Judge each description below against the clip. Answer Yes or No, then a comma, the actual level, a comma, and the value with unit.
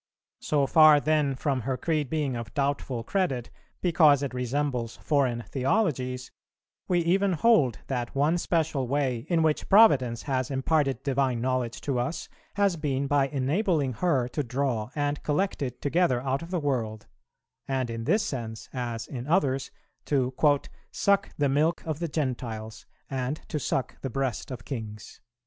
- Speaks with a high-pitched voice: No, low, 135 Hz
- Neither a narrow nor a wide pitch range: Yes, average, 3.6 semitones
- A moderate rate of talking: Yes, average, 160 wpm